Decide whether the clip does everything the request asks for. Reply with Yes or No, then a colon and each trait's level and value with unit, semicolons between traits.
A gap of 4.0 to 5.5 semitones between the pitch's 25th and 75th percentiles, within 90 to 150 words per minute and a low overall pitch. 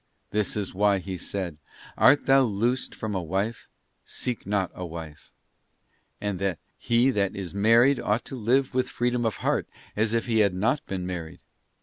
No: average, 4.3 semitones; average, 165 wpm; low, 105 Hz